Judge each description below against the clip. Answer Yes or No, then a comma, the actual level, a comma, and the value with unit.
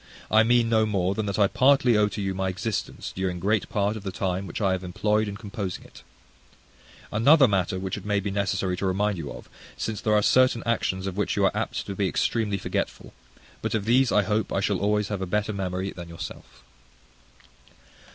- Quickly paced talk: Yes, fast, 215 wpm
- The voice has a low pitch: Yes, low, 100 Hz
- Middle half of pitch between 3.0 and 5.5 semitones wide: No, narrow, 2.4 semitones